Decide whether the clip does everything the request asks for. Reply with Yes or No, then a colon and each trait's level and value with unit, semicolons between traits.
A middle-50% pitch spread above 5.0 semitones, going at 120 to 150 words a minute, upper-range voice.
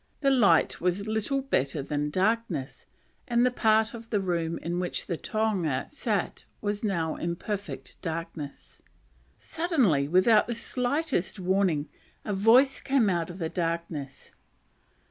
Yes: wide, 5.5 semitones; average, 140 wpm; high, 195 Hz